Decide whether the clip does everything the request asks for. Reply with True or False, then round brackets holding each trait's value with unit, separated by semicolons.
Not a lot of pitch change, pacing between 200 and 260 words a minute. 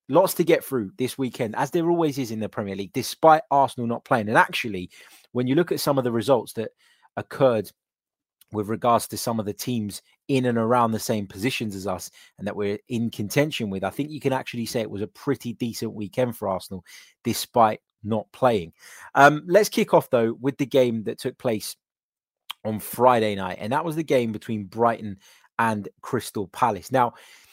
False (4.5 semitones; 205 wpm)